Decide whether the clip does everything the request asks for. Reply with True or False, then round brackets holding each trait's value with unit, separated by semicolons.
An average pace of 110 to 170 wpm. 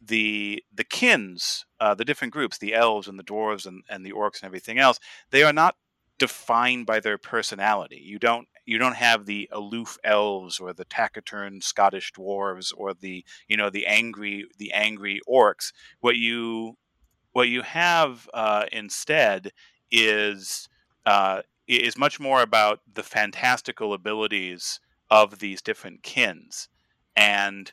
True (150 wpm)